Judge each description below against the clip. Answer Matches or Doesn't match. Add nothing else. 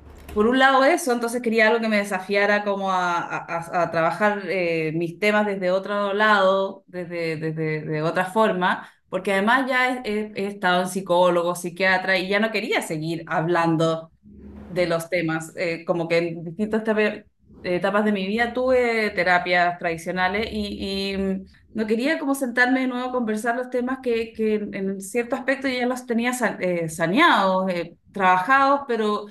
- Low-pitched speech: Doesn't match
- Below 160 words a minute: Doesn't match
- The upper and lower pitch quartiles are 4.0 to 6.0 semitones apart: Matches